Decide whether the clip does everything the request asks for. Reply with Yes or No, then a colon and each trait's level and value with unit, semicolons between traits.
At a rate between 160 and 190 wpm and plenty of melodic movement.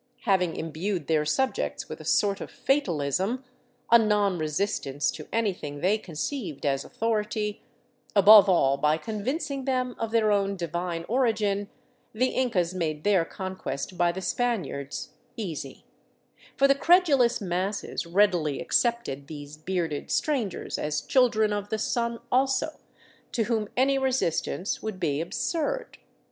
No: slow, 135 wpm; wide, 6.0 semitones